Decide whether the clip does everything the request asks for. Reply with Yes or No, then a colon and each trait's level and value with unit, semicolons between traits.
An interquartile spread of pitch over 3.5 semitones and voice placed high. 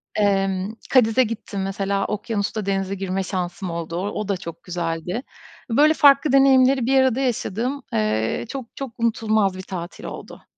Yes: average, 5.0 semitones; high, 200 Hz